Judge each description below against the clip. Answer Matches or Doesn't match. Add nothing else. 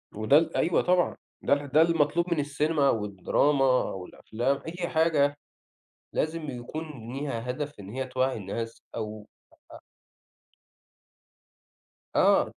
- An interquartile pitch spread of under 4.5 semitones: Doesn't match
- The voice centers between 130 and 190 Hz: Matches